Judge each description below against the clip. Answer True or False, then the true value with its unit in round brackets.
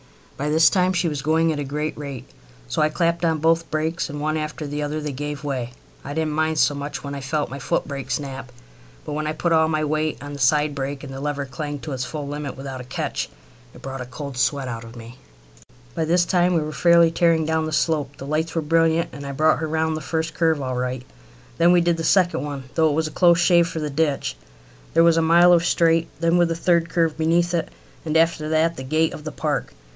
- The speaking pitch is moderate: True (155 Hz)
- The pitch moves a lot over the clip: False (2.5 semitones)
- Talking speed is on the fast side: True (250 wpm)